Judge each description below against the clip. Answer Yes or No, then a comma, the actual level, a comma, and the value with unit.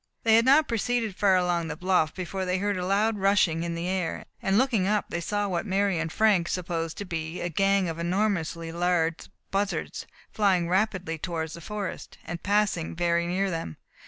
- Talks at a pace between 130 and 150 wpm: No, average, 190 wpm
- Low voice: No, medium, 185 Hz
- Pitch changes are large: No, average, 3.2 semitones